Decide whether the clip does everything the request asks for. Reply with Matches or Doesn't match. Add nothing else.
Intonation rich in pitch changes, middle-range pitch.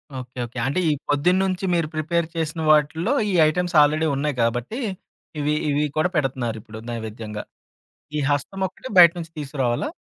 Doesn't match